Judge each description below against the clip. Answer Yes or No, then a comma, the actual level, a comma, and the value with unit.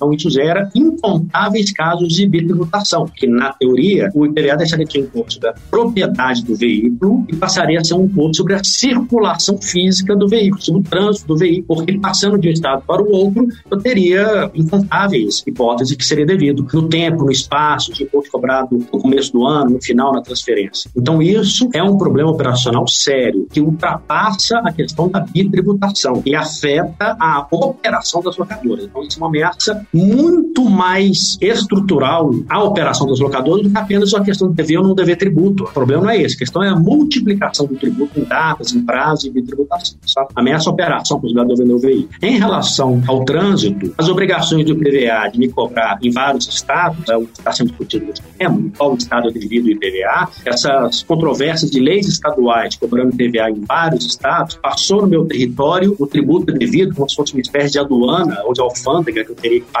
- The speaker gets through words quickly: Yes, fast, 200 wpm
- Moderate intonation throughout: No, wide, 6.3 semitones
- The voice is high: No, medium, 165 Hz